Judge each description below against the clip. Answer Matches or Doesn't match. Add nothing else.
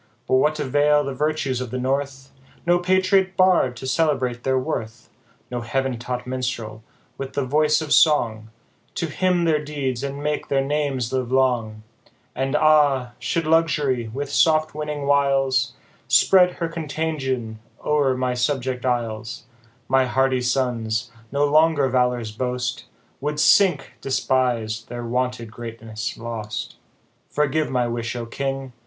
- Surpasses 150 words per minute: Doesn't match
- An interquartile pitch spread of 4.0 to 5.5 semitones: Doesn't match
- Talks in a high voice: Doesn't match